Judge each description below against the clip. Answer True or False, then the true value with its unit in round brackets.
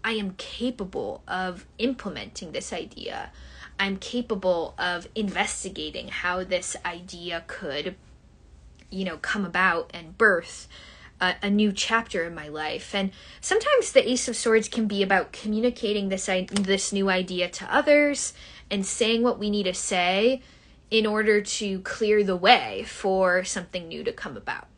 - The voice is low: False (200 Hz)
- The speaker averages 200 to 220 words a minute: False (155 wpm)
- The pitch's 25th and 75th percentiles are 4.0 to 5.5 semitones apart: False (3.4 semitones)